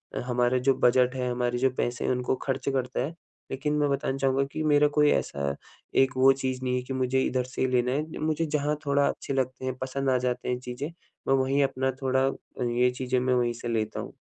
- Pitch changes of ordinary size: No, narrow, 1.5 semitones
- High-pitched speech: No, low, 130 Hz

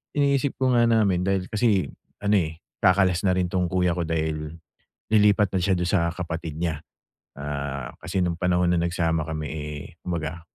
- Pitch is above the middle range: No, very low, 90 Hz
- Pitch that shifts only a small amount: No, average, 3.3 semitones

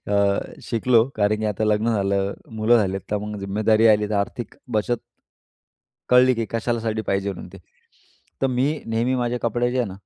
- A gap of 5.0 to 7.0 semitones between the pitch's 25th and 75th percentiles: No, average, 2.8 semitones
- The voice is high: No, low, 110 Hz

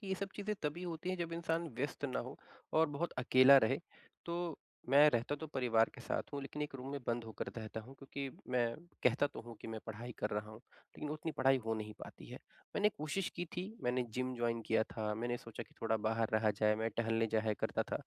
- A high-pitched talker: No, low, 130 Hz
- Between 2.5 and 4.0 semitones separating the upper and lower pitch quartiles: No, average, 5.1 semitones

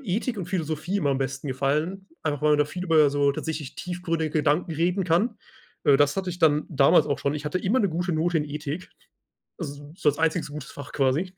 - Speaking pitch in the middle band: Yes, medium, 155 Hz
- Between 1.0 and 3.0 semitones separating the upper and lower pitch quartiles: No, average, 3.5 semitones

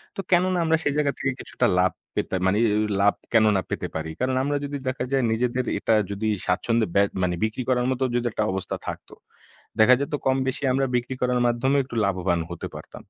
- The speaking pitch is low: Yes, low, 125 Hz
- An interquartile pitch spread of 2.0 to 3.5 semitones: No, average, 4.6 semitones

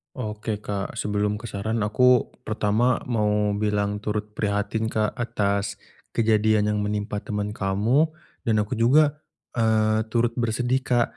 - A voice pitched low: Yes, low, 105 Hz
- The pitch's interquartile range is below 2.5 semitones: Yes, narrow, 1.9 semitones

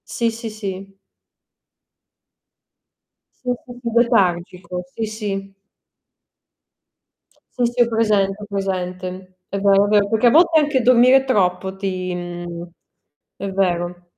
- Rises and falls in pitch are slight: No, average, 3.8 semitones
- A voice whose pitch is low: No, high, 195 Hz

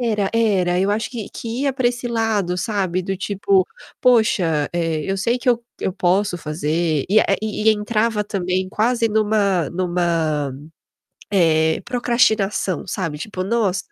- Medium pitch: No, high, 195 Hz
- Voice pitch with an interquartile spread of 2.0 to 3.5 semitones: No, average, 4.0 semitones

